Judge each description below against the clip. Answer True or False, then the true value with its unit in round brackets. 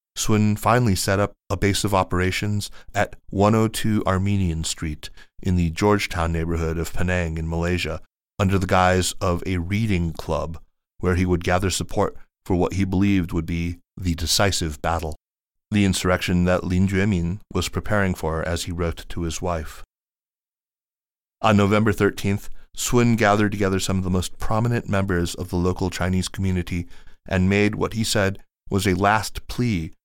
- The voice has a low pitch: True (90 Hz)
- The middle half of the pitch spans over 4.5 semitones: False (2.8 semitones)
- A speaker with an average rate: True (160 wpm)